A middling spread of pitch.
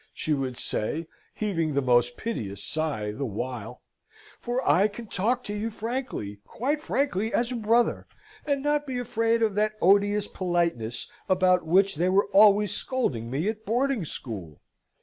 No: wide, 8.6 semitones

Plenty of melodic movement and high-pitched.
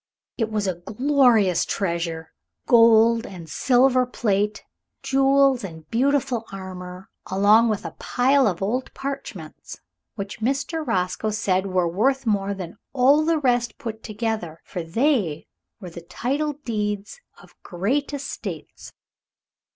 Yes: wide, 5.9 semitones; high, 220 Hz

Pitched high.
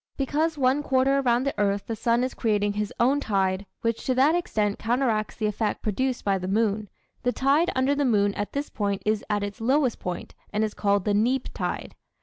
Yes: high, 225 Hz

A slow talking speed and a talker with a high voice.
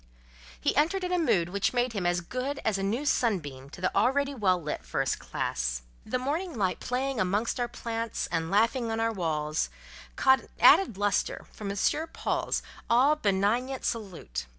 No: average, 175 wpm; high, 220 Hz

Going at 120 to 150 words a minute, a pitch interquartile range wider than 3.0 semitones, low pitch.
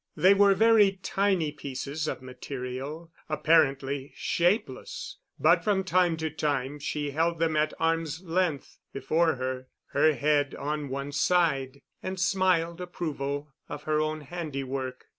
No: slow, 135 wpm; average, 3.6 semitones; medium, 155 Hz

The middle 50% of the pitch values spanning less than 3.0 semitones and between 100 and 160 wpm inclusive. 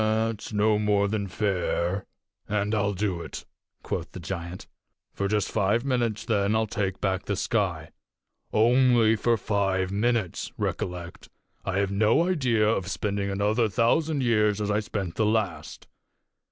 Yes: narrow, 2.4 semitones; average, 150 wpm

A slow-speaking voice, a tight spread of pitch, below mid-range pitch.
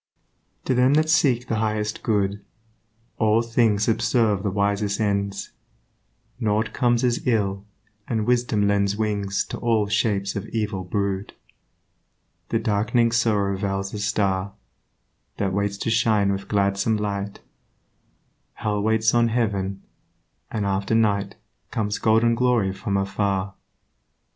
Yes: slow, 130 wpm; narrow, 2.2 semitones; low, 105 Hz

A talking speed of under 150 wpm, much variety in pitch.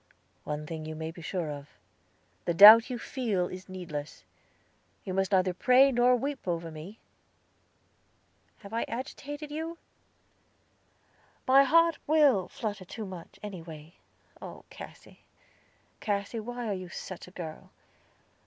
Yes: slow, 135 wpm; wide, 6.4 semitones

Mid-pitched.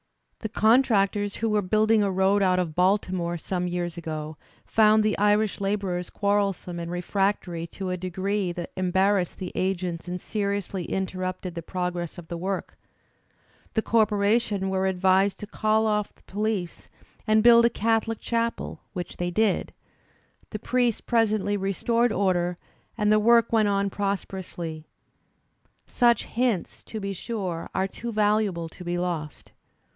No: high, 195 Hz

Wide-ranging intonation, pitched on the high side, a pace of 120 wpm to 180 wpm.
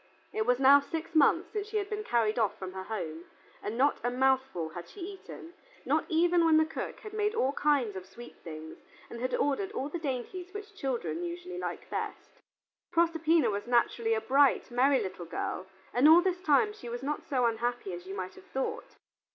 No: wide, 7.3 semitones; very high, 270 Hz; fast, 205 wpm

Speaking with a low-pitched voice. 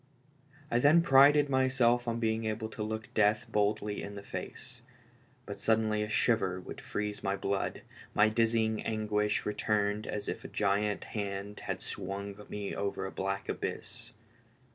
Yes: low, 105 Hz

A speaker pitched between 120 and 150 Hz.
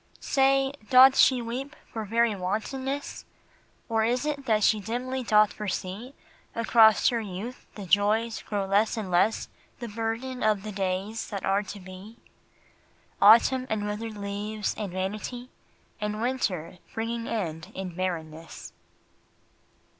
No: high, 215 Hz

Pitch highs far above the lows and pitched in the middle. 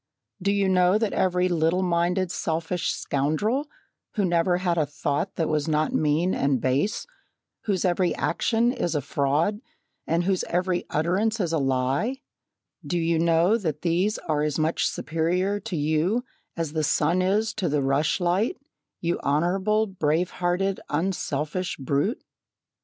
No: average, 3.7 semitones; medium, 175 Hz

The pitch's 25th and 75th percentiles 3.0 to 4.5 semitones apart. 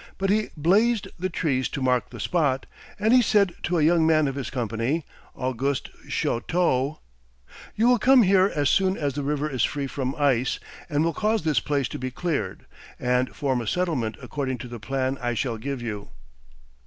No: wide, 5.5 semitones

